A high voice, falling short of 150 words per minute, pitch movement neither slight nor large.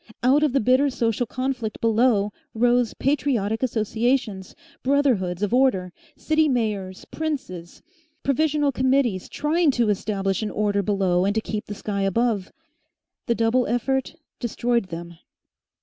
Yes: high, 230 Hz; slow, 135 wpm; average, 4.6 semitones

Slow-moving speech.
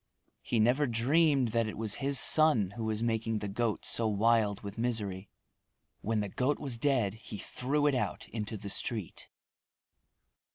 No: average, 165 wpm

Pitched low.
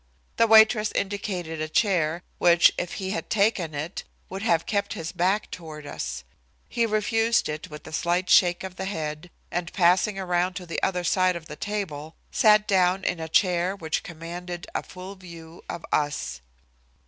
No: medium, 180 Hz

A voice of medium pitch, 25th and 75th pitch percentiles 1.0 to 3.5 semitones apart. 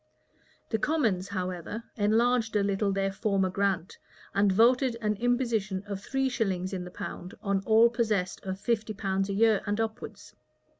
No: high, 205 Hz; average, 2.9 semitones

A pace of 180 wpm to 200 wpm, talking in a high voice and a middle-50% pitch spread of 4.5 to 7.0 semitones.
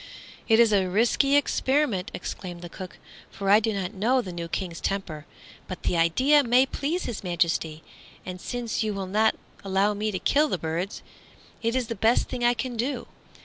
Yes: average, 190 wpm; high, 210 Hz; average, 5.0 semitones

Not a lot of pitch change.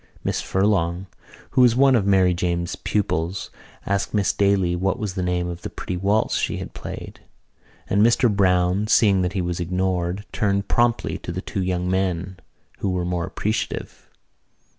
Yes: narrow, 2.3 semitones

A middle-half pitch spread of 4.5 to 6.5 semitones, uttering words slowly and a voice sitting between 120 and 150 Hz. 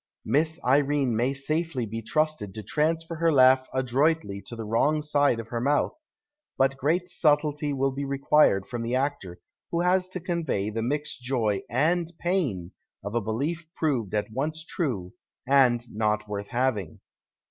No: average, 5.2 semitones; average, 160 wpm; low, 135 Hz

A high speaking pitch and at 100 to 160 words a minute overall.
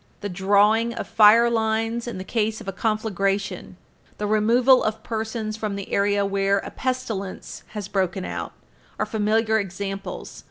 Yes: high, 215 Hz; average, 155 wpm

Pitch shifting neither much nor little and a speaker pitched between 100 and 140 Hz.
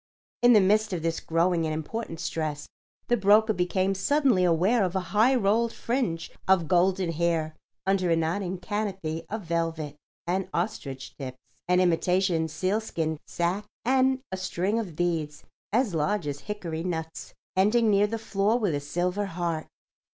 No: average, 4.0 semitones; medium, 180 Hz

